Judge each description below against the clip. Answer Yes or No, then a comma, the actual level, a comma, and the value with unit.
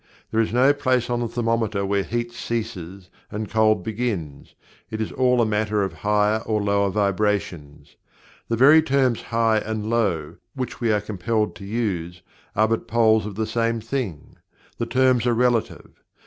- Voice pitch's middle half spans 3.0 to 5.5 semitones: No, narrow, 2.6 semitones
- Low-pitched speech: Yes, low, 110 Hz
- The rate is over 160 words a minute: Yes, average, 170 wpm